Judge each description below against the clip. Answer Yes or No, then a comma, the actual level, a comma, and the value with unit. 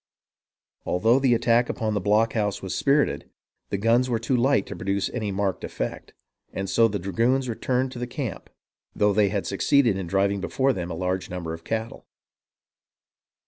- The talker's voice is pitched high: No, low, 110 Hz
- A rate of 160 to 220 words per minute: Yes, average, 170 wpm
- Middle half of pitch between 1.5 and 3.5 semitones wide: No, average, 4.0 semitones